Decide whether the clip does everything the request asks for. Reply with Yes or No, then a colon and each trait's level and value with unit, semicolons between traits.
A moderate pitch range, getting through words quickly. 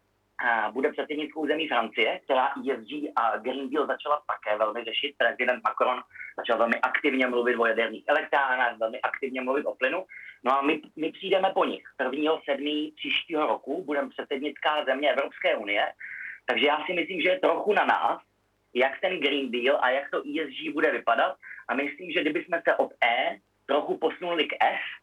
Yes: average, 4.3 semitones; fast, 175 wpm